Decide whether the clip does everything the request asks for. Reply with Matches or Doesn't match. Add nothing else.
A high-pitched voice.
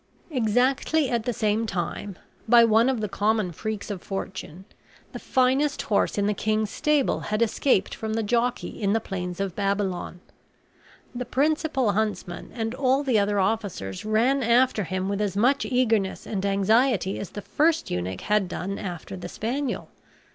Matches